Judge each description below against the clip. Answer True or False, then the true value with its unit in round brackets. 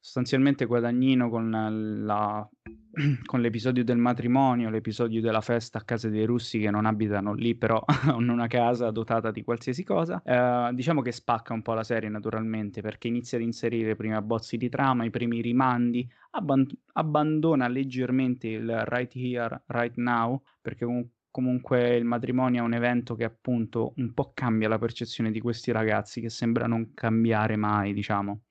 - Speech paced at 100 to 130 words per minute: False (165 wpm)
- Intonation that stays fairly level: True (1.9 semitones)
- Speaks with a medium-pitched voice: False (120 Hz)